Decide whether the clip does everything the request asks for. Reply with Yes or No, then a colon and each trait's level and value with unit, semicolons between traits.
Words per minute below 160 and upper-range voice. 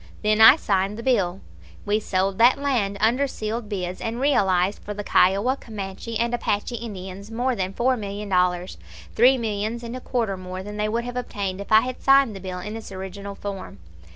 No: average, 200 wpm; high, 210 Hz